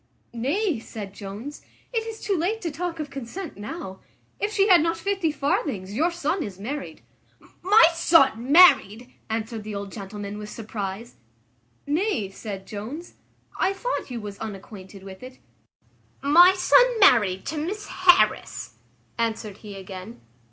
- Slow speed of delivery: No, average, 145 wpm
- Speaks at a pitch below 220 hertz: No, very high, 255 Hz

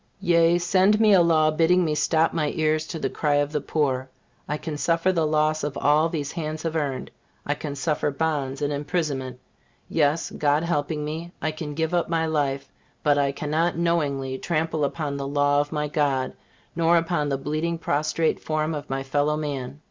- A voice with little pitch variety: Yes, narrow, 2.3 semitones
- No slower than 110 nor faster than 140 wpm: No, average, 195 wpm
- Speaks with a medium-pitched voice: Yes, medium, 155 Hz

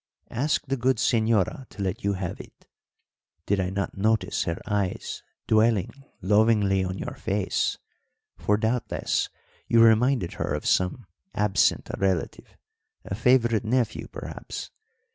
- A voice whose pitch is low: Yes, low, 105 Hz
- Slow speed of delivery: Yes, slow, 130 wpm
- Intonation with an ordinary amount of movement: Yes, average, 3.3 semitones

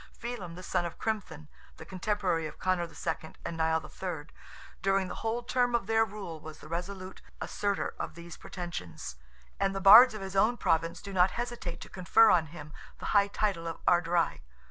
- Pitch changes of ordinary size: Yes, average, 3.7 semitones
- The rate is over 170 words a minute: Yes, average, 190 wpm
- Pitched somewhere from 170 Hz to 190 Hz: Yes, medium, 185 Hz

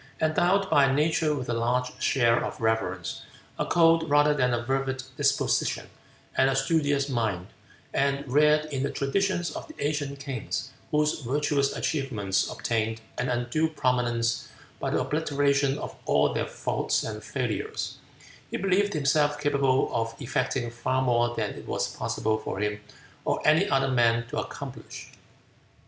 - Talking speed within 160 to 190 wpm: No, average, 150 wpm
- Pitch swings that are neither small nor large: Yes, average, 3.9 semitones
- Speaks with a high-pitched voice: No, low, 135 Hz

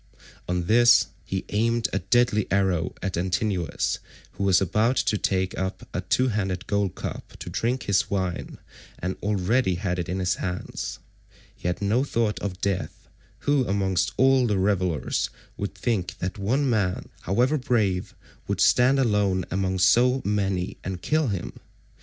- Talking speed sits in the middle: Yes, average, 155 wpm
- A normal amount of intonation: Yes, average, 4.1 semitones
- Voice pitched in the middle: No, low, 100 Hz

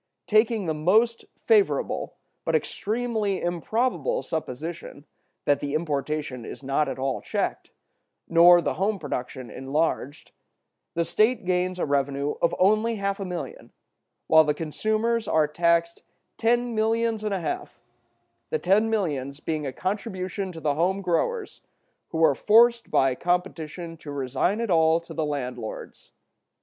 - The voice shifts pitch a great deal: Yes, wide, 6.4 semitones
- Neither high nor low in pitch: Yes, medium, 175 Hz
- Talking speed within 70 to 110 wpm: No, average, 140 wpm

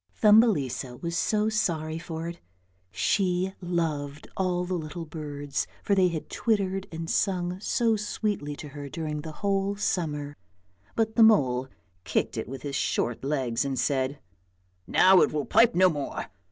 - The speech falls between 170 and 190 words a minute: No, average, 160 wpm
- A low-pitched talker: No, medium, 165 Hz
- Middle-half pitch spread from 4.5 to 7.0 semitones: Yes, average, 5.1 semitones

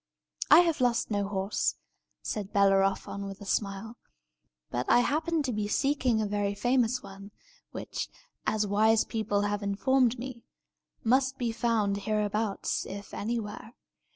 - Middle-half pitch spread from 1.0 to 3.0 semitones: No, average, 3.4 semitones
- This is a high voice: Yes, high, 215 Hz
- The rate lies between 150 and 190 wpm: No, average, 140 wpm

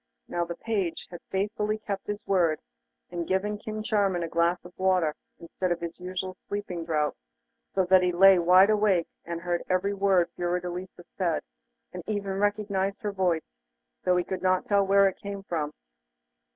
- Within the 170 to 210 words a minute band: Yes, average, 175 wpm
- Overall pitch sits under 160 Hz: No, medium, 185 Hz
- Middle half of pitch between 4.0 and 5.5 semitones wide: No, narrow, 2.4 semitones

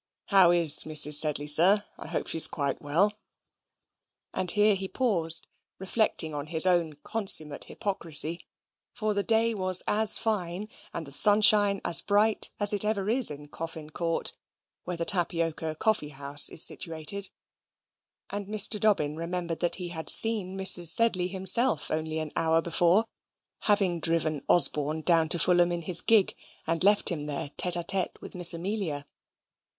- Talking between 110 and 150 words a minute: No, average, 160 wpm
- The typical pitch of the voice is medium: Yes, medium, 175 Hz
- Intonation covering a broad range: No, average, 4.2 semitones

